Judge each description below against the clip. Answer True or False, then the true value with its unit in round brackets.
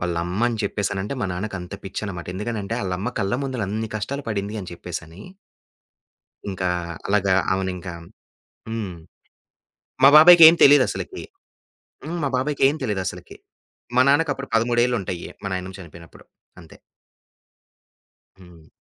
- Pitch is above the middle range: False (100 Hz)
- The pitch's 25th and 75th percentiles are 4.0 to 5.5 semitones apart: True (5.1 semitones)